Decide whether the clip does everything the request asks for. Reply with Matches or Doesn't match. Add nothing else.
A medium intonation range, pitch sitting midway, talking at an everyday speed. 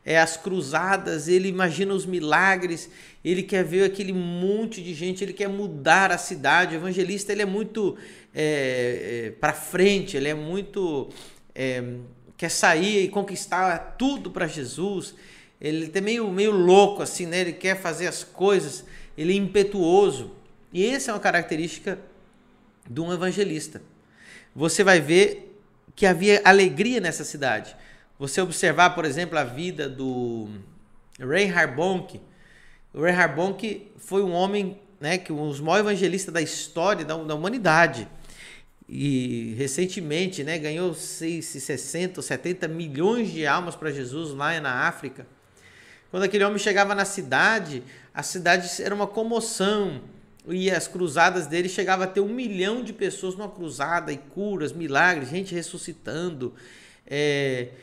Matches